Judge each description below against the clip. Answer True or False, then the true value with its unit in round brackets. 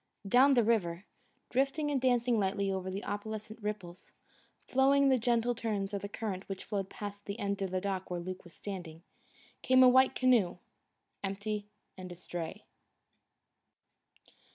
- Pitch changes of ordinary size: True (4.2 semitones)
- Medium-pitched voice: False (205 Hz)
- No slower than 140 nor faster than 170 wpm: True (155 wpm)